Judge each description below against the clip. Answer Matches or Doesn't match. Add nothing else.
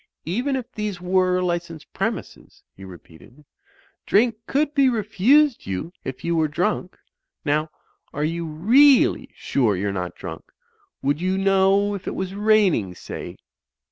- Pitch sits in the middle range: Matches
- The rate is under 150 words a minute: Matches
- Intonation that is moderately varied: Doesn't match